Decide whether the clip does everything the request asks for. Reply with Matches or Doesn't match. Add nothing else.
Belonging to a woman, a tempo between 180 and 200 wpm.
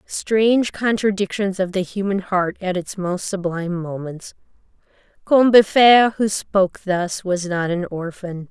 Doesn't match